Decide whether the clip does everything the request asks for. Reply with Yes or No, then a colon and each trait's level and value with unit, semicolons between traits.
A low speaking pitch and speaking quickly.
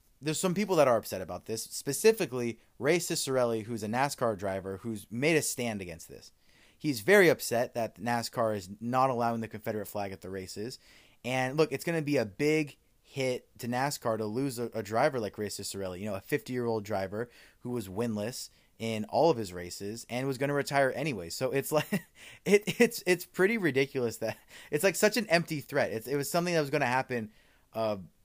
Yes: low, 120 Hz; fast, 210 wpm